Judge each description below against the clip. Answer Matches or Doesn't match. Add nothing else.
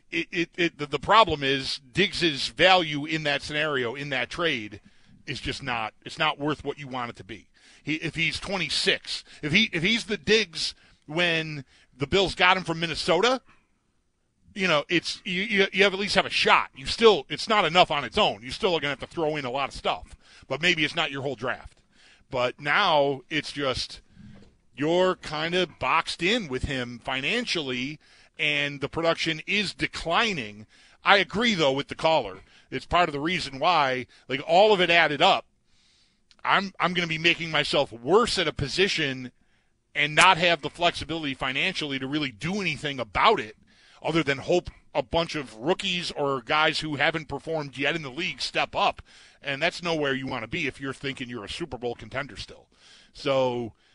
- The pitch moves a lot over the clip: Doesn't match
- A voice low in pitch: Doesn't match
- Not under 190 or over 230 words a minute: Matches